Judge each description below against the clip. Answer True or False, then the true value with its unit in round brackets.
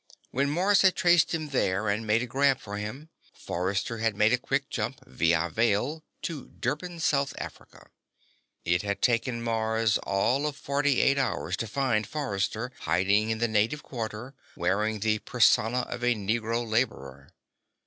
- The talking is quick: False (160 wpm)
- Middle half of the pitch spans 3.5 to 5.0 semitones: True (4.5 semitones)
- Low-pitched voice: True (115 Hz)